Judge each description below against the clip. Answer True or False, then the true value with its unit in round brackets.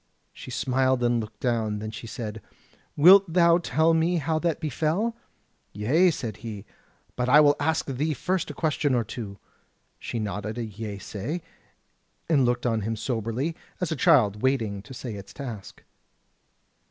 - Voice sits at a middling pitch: False (125 Hz)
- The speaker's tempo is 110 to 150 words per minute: False (160 wpm)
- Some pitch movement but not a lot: False (6.4 semitones)